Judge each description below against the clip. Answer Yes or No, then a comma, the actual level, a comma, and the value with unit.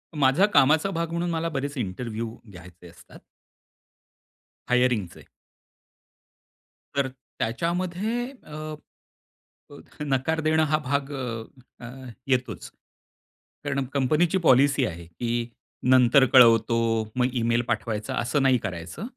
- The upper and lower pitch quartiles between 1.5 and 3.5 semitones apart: No, average, 5.0 semitones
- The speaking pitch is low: Yes, low, 130 Hz